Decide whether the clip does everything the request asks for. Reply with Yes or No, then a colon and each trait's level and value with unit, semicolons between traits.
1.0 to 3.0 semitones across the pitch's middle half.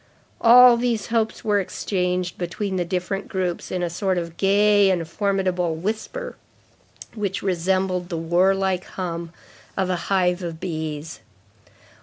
Yes: narrow, 2.4 semitones